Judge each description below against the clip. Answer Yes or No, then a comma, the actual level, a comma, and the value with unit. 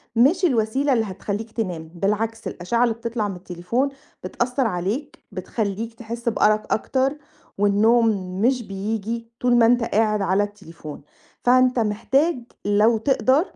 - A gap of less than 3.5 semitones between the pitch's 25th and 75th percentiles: Yes, average, 3.1 semitones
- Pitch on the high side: Yes, high, 225 Hz